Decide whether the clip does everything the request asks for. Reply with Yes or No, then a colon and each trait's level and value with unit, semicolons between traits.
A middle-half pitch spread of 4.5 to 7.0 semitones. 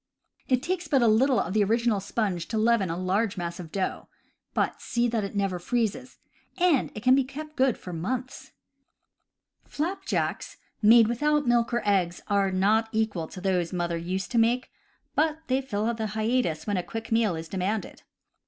Yes: average, 4.8 semitones